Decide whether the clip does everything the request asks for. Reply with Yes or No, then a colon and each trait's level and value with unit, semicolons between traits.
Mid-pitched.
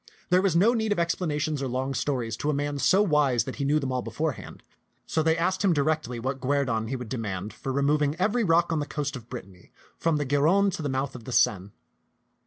Yes: medium, 145 Hz